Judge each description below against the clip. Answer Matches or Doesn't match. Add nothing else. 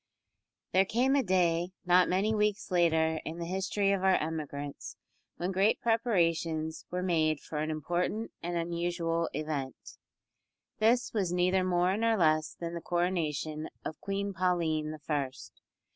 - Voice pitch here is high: Doesn't match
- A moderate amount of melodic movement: Matches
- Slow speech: Doesn't match